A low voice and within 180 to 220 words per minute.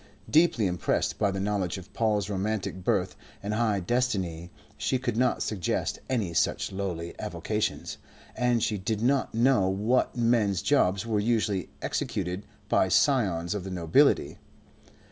No: low, 105 Hz; average, 145 wpm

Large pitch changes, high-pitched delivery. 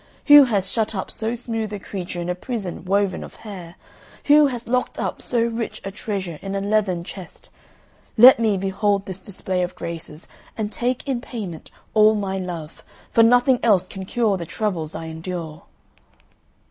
No: average, 4.0 semitones; high, 200 Hz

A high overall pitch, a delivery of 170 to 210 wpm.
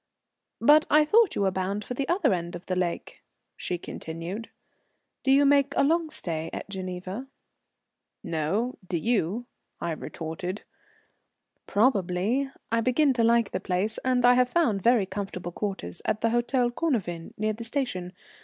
No: high, 215 Hz; average, 160 wpm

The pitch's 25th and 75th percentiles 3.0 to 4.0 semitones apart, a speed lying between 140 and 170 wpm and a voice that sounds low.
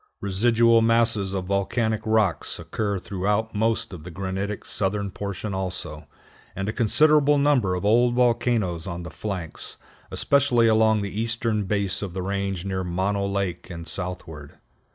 Yes: average, 3.3 semitones; average, 150 wpm; low, 100 Hz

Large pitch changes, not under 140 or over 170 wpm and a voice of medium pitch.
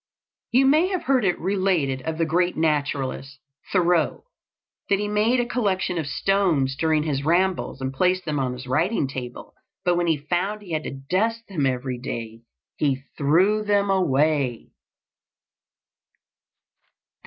Yes: wide, 6.2 semitones; average, 150 wpm; medium, 165 Hz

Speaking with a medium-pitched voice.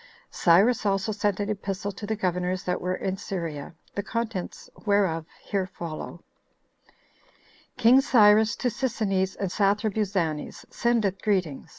No: high, 200 Hz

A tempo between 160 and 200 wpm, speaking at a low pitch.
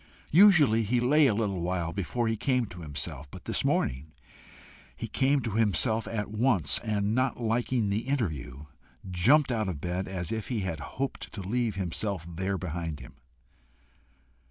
Yes: average, 165 wpm; low, 105 Hz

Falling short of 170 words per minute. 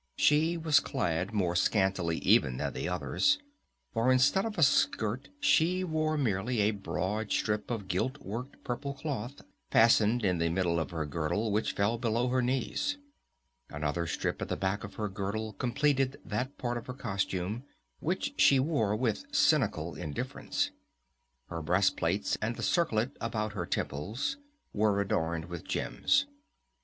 Yes: average, 160 wpm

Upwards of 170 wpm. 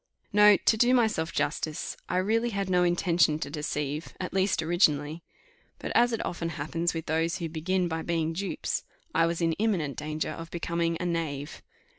Yes: average, 180 wpm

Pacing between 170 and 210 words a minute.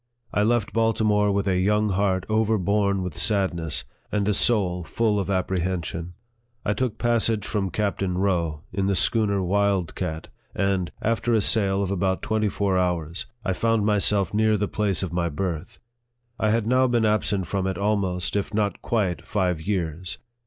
Yes: average, 175 wpm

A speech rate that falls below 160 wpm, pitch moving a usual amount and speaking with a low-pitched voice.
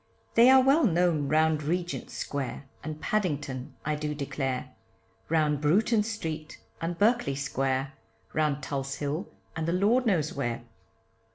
No: average, 140 wpm; average, 4.4 semitones; medium, 155 Hz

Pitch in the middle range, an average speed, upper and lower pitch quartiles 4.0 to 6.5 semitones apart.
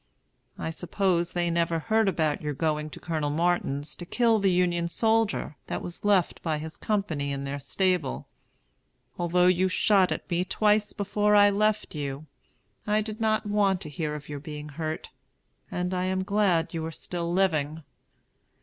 Yes: medium, 175 Hz; average, 170 wpm; average, 4.5 semitones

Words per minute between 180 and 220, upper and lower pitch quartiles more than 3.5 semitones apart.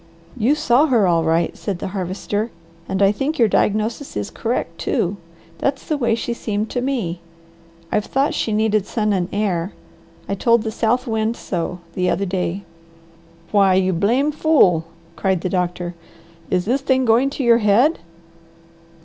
No: average, 165 wpm; average, 4.7 semitones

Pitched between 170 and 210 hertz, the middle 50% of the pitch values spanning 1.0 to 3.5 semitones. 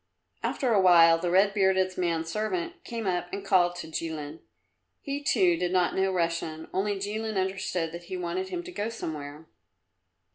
Yes: medium, 185 Hz; average, 2.9 semitones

